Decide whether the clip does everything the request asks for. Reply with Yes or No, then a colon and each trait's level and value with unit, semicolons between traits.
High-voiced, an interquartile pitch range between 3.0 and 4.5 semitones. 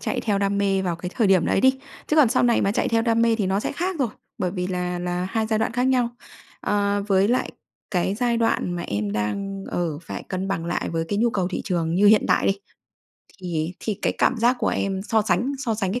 Yes: high, 200 Hz; average, 4.2 semitones